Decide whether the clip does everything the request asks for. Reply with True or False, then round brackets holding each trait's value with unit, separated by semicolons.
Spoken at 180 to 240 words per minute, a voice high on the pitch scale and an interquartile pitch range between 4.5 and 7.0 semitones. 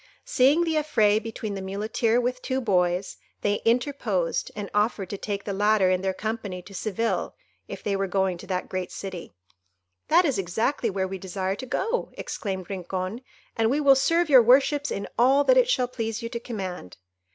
True (185 wpm; 215 Hz; 4.8 semitones)